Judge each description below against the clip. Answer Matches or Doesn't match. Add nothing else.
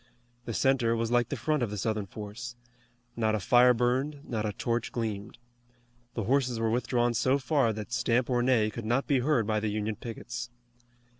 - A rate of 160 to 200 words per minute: Matches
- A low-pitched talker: Matches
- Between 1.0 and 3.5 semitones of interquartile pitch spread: Matches